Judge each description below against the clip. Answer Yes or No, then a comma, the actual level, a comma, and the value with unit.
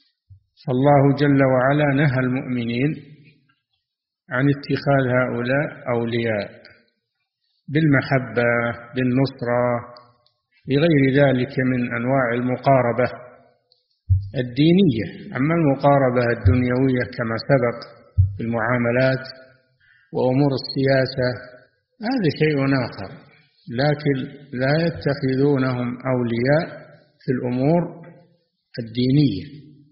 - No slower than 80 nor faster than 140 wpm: No, average, 70 wpm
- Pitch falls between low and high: No, low, 130 Hz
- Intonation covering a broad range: No, average, 2.7 semitones